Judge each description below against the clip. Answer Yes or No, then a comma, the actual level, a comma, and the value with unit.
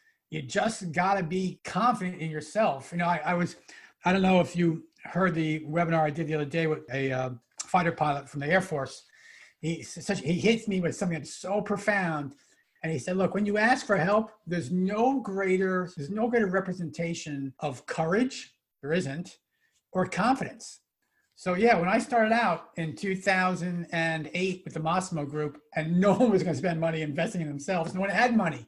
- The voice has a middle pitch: Yes, medium, 180 Hz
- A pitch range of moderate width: Yes, average, 3.7 semitones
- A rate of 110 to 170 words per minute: No, average, 190 wpm